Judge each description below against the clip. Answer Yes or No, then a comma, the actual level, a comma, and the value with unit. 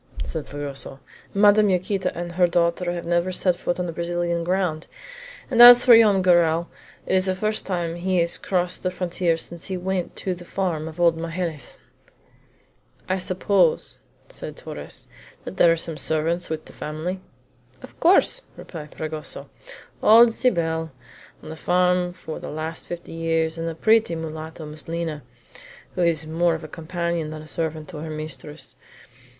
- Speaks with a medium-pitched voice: Yes, medium, 170 Hz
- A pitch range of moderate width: No, narrow, 2.3 semitones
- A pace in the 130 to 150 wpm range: No, average, 165 wpm